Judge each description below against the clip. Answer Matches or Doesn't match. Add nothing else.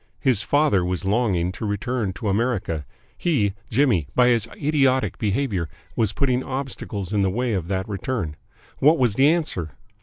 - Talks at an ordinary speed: Matches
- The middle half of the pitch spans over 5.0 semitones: Matches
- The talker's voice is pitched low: Matches